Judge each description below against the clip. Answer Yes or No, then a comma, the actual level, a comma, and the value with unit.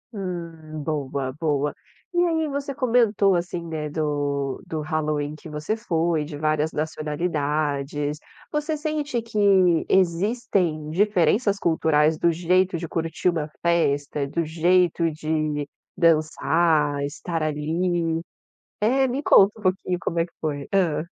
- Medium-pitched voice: Yes, medium, 165 Hz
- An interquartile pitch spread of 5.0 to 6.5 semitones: No, average, 3.5 semitones